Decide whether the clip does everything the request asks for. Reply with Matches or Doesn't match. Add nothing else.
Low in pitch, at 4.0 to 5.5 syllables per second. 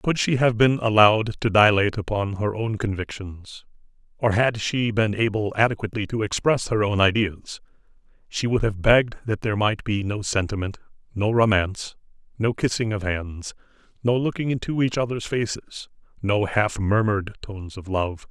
Matches